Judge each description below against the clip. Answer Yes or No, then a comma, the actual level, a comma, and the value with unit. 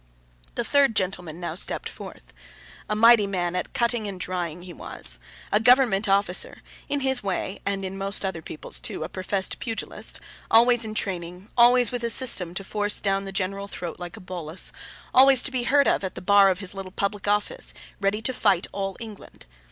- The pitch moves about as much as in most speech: Yes, average, 3.8 semitones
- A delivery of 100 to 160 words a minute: No, average, 195 wpm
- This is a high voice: Yes, high, 200 Hz